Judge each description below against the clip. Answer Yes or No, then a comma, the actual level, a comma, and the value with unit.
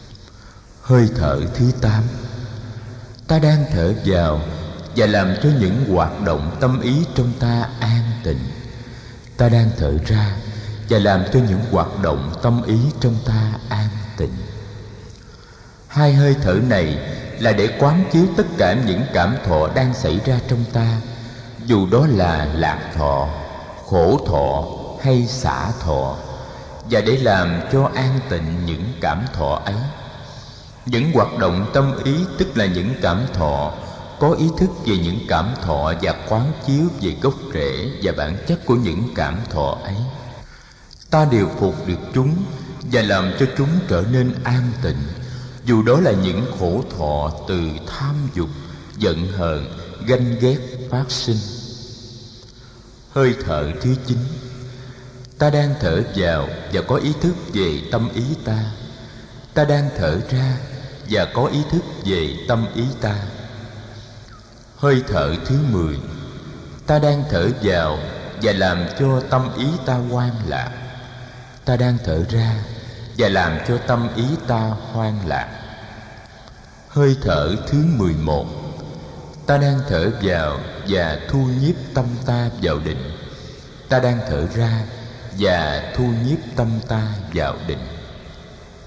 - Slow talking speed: Yes, slow, 145 wpm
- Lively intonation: No, average, 4.9 semitones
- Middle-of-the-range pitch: No, low, 115 Hz